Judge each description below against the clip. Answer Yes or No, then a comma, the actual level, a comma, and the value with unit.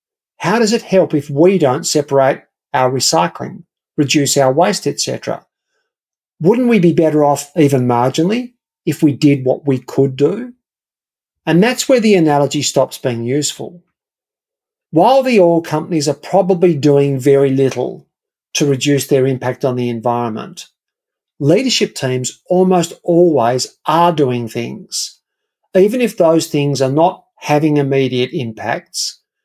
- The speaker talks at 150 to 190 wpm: No, average, 140 wpm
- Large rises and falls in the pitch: Yes, wide, 5.9 semitones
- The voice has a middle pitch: Yes, medium, 150 Hz